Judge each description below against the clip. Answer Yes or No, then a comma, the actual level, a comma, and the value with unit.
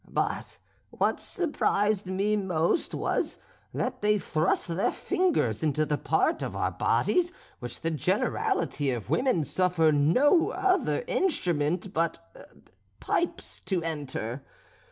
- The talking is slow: Yes, slow, 120 wpm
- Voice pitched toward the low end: No, medium, 175 Hz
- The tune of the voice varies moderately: No, wide, 6.2 semitones